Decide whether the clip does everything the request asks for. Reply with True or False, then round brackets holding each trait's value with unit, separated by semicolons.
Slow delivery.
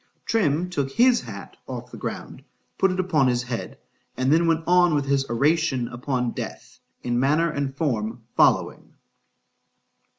False (145 wpm)